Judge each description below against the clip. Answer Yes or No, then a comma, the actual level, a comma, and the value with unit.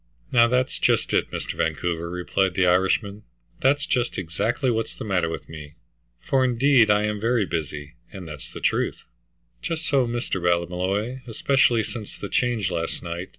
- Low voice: Yes, low, 105 Hz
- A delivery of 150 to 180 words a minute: Yes, average, 165 wpm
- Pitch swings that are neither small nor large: No, wide, 5.7 semitones